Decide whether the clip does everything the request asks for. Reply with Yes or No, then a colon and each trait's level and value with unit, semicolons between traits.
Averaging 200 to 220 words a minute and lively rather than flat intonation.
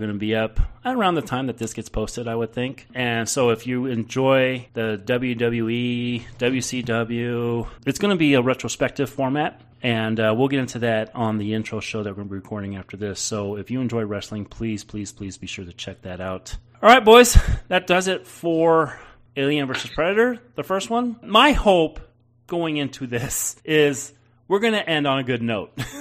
No: fast, 205 wpm; average, 4.3 semitones